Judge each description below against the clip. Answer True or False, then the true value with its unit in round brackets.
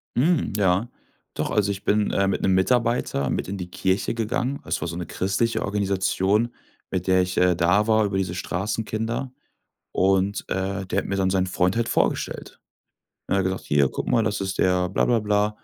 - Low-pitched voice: True (95 Hz)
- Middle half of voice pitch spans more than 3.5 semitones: False (2.6 semitones)